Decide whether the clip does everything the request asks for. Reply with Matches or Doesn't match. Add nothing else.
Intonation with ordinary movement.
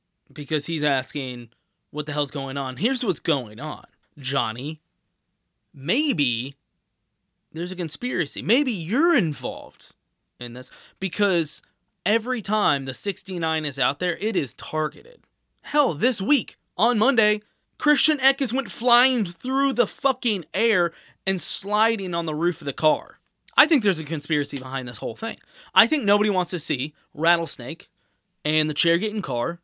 Doesn't match